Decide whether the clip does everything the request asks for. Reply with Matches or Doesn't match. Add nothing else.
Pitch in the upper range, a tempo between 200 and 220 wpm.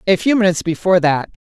Doesn't match